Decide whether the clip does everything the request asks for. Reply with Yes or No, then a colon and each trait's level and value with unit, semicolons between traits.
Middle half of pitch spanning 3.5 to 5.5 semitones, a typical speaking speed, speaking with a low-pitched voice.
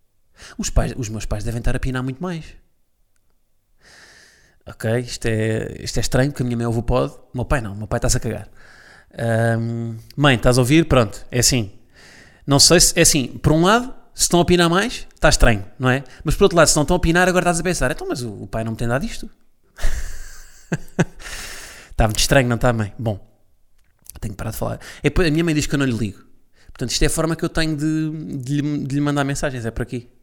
No: average, 5.2 semitones; fast, 240 wpm; low, 125 Hz